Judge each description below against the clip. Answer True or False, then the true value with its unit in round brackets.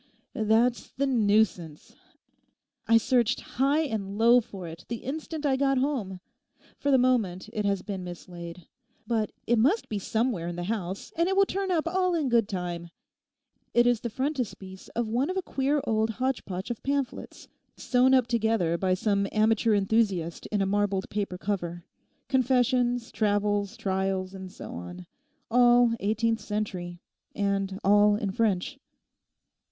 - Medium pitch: False (220 Hz)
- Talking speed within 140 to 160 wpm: True (150 wpm)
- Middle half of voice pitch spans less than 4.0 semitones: False (4.6 semitones)